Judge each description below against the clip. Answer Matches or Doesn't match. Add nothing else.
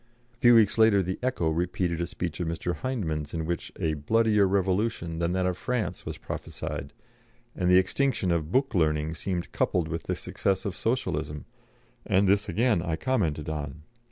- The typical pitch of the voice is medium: Doesn't match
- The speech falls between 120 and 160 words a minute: Doesn't match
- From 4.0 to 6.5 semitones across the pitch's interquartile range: Matches